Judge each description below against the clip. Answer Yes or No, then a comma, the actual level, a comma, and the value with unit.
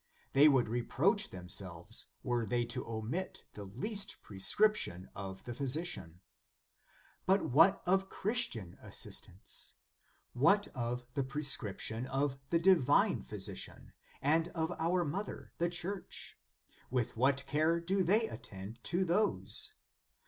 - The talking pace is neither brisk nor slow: No, slow, 125 wpm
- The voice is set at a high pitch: No, medium, 140 Hz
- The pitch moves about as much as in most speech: No, wide, 7.6 semitones